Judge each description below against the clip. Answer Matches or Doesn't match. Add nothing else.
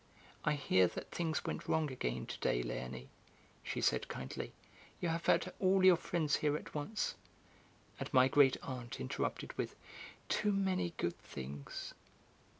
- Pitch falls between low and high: Matches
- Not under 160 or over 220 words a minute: Doesn't match